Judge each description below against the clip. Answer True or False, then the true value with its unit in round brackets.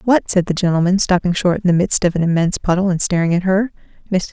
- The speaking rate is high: True (250 wpm)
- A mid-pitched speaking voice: True (180 Hz)